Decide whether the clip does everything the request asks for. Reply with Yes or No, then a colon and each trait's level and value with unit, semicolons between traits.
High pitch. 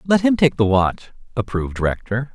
No: low, 125 Hz